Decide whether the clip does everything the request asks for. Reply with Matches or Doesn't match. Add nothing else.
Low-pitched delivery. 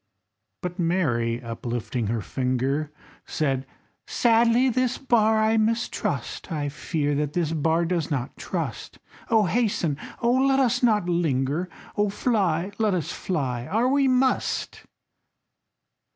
Doesn't match